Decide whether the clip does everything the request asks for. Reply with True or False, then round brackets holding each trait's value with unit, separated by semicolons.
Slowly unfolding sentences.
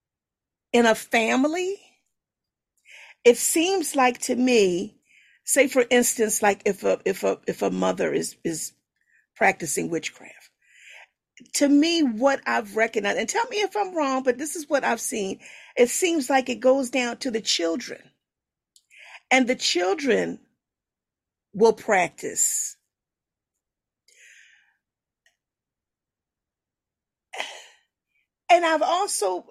True (115 wpm)